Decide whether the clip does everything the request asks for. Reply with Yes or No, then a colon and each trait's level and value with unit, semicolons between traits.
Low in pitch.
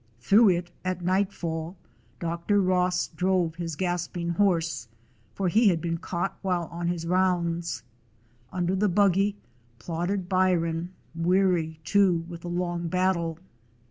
No: medium, 175 Hz